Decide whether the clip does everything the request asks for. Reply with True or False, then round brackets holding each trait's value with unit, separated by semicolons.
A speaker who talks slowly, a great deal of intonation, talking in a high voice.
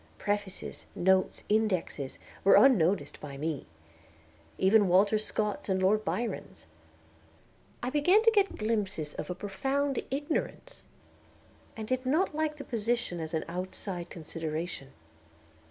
True (120 wpm; 6.4 semitones; 205 Hz)